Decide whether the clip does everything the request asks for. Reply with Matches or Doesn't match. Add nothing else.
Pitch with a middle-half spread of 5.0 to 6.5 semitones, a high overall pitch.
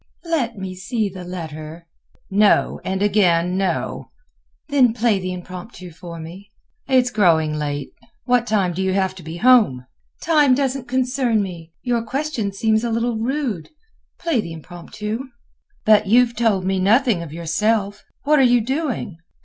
Matches